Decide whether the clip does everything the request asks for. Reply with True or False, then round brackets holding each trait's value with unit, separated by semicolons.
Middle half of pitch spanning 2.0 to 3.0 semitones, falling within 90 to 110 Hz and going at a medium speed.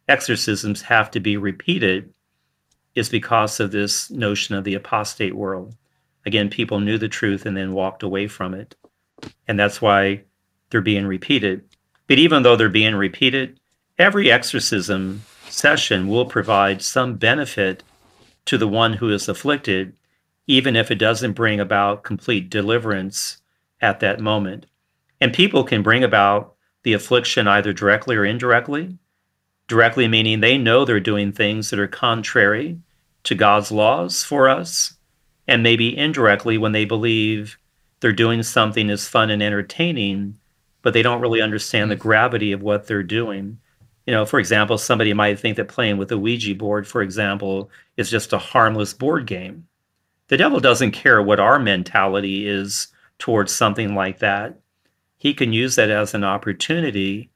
True (2.7 semitones; 105 Hz; 160 wpm)